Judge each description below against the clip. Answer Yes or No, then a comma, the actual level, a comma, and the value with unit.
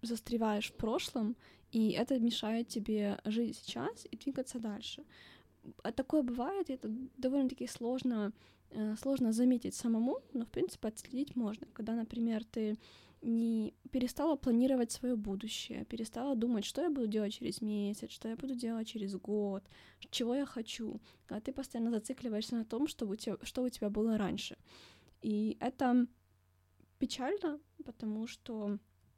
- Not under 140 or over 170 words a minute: Yes, average, 145 wpm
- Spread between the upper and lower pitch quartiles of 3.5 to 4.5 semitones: No, average, 3.0 semitones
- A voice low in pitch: No, high, 235 Hz